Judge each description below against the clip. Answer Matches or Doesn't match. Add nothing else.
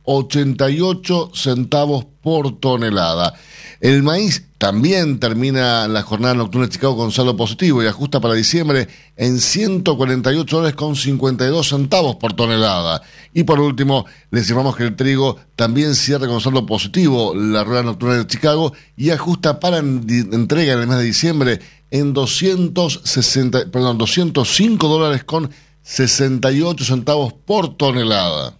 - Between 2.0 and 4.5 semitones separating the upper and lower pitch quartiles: Matches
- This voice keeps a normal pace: Matches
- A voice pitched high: Doesn't match